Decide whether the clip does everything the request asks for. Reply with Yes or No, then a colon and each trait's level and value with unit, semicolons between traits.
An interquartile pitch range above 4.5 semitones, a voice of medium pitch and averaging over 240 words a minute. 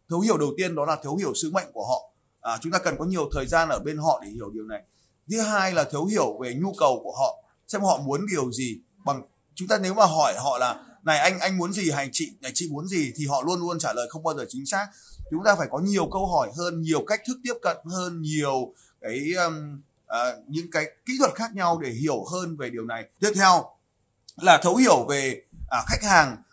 Yes: average, 5.1 semitones; medium, 165 Hz; fast, 250 wpm